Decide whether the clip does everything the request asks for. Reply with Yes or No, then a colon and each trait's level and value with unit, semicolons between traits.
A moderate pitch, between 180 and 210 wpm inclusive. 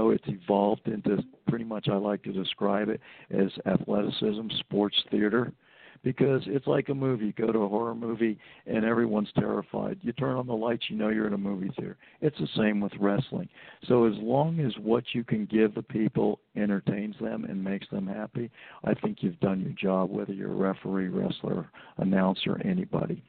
No: low, 110 Hz; average, 190 wpm